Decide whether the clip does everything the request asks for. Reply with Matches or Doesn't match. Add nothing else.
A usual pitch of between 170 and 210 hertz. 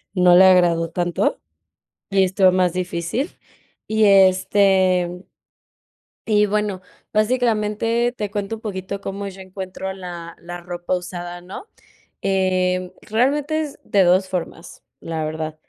Matches